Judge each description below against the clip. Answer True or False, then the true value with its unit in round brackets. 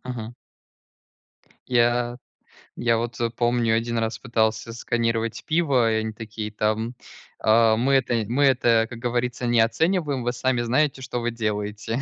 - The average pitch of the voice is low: True (120 Hz)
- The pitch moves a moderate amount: False (1.6 semitones)